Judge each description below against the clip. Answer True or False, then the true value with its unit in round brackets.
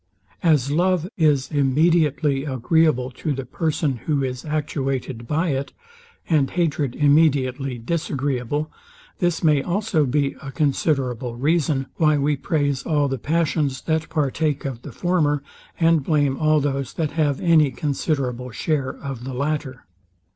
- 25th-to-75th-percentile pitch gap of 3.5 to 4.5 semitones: False (2.8 semitones)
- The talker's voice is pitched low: False (145 Hz)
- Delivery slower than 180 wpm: True (140 wpm)